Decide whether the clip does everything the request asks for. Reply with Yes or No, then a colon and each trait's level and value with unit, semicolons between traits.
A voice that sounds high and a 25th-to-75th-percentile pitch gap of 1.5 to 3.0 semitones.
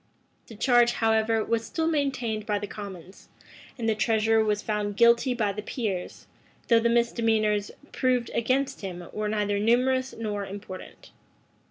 Yes: high, 220 Hz; narrow, 2.4 semitones